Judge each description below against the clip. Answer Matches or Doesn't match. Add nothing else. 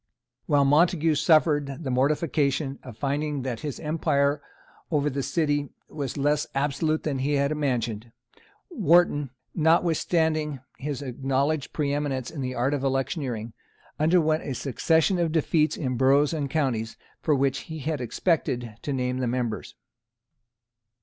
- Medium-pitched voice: Matches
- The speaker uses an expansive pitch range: Doesn't match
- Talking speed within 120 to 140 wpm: Matches